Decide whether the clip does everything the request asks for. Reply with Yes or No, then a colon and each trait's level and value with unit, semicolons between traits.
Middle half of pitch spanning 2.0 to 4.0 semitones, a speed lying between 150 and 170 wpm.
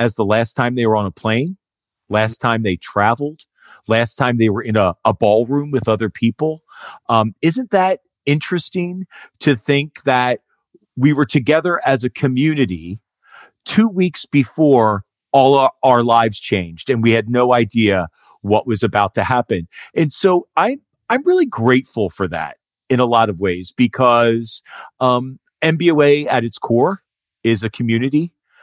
No: average, 4.8 semitones; average, 160 wpm